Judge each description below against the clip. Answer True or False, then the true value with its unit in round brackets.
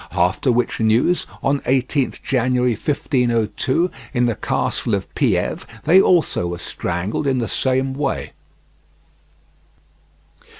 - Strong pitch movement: False (3.3 semitones)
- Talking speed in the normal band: False (115 wpm)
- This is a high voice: False (125 Hz)